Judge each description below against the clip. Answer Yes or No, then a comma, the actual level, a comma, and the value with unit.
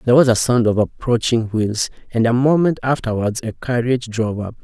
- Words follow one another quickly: No, average, 195 wpm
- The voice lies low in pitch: Yes, low, 120 Hz